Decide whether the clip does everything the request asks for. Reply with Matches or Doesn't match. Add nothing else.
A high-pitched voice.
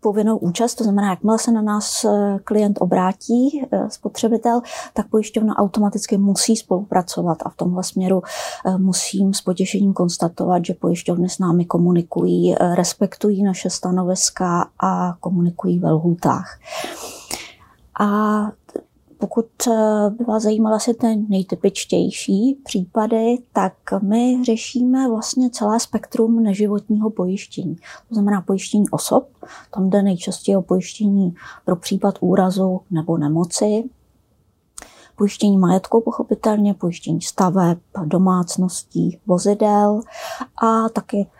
Matches